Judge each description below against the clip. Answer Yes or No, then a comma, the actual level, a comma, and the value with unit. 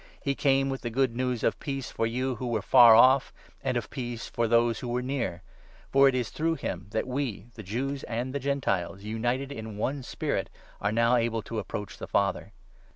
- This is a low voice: Yes, low, 120 Hz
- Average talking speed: No, fast, 235 wpm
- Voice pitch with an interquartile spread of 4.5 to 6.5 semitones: No, average, 3.0 semitones